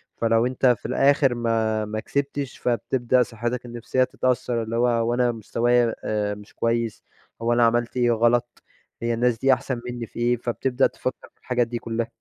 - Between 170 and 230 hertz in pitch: No, low, 120 Hz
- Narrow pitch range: Yes, narrow, 1.2 semitones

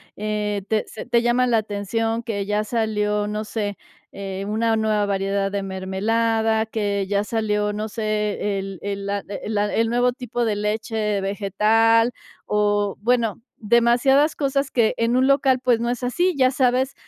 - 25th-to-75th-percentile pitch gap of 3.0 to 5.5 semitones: No, narrow, 2.4 semitones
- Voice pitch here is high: Yes, high, 215 Hz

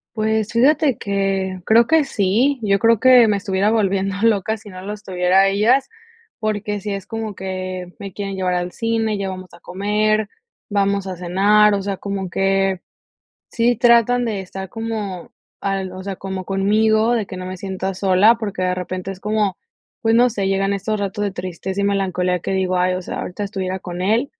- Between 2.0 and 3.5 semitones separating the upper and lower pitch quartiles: Yes, narrow, 2.4 semitones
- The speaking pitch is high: Yes, high, 200 Hz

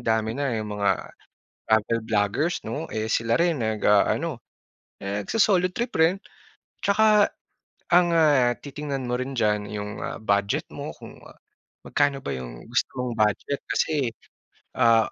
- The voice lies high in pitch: No, low, 120 Hz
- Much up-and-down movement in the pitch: Yes, wide, 6.7 semitones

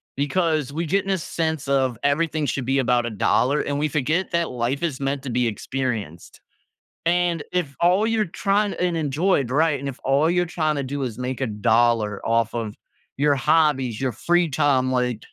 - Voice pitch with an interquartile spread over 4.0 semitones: Yes, average, 4.7 semitones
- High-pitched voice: No, medium, 140 Hz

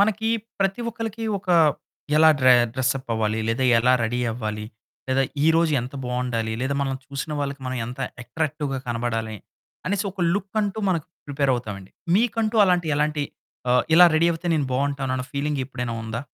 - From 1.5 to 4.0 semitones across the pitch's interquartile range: No, wide, 5.5 semitones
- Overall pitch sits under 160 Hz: Yes, medium, 140 Hz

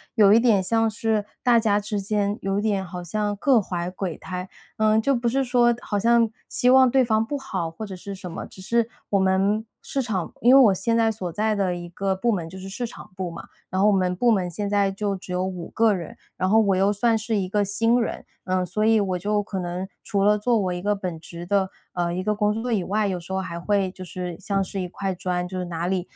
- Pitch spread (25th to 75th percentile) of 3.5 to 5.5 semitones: No, average, 3.1 semitones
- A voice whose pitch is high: Yes, high, 200 Hz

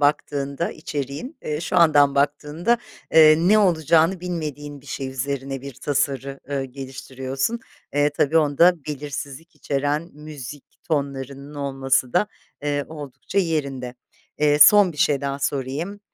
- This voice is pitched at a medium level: Yes, medium, 145 Hz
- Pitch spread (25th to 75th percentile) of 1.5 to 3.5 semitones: Yes, narrow, 2.6 semitones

